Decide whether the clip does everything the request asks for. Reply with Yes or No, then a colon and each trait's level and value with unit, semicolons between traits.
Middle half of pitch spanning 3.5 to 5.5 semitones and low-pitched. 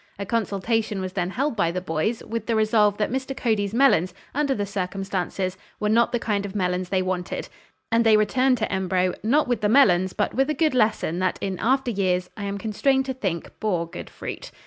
No: average, 4.0 semitones; high, 210 Hz